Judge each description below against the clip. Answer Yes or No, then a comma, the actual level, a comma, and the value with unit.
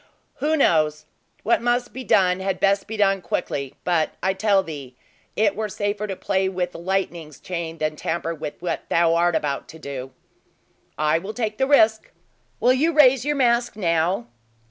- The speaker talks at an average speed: Yes, average, 175 wpm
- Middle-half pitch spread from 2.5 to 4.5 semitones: No, average, 5.1 semitones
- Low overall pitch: No, high, 190 Hz